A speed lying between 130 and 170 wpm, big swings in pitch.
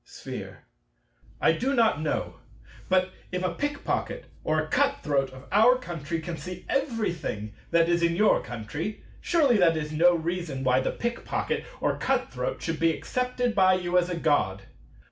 No: average, 180 wpm; wide, 6.2 semitones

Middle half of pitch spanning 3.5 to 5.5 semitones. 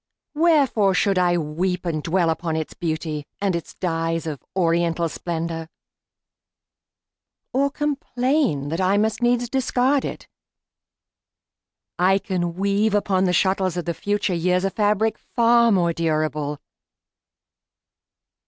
Yes: average, 4.6 semitones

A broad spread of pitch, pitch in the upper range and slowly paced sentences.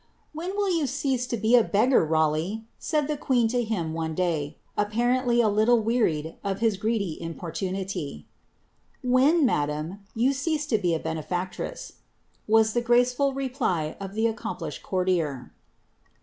Yes: wide, 6.7 semitones; high, 220 Hz; slow, 130 wpm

